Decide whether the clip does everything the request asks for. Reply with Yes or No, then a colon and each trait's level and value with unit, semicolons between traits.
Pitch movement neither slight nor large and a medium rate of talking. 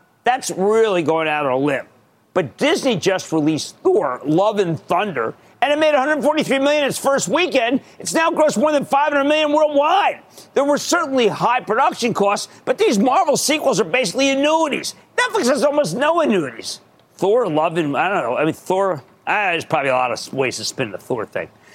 No: wide, 7.1 semitones; average, 195 wpm